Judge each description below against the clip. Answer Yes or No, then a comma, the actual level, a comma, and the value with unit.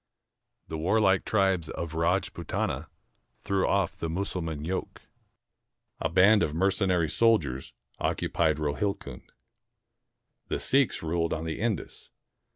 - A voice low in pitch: Yes, very low, 90 Hz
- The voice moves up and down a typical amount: Yes, average, 3.5 semitones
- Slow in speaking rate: Yes, slow, 110 wpm